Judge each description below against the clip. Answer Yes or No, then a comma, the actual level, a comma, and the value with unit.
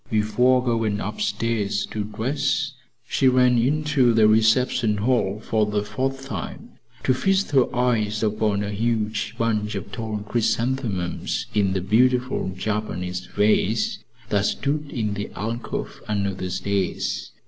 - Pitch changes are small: No, average, 3.4 semitones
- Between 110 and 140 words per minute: Yes, slow, 135 wpm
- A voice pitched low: Yes, low, 110 Hz